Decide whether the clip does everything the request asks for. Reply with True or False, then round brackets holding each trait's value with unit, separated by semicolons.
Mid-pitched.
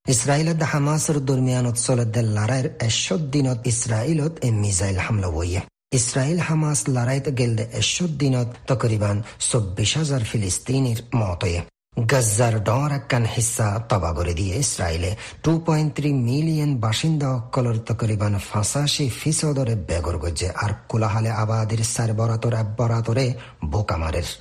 False (120 Hz)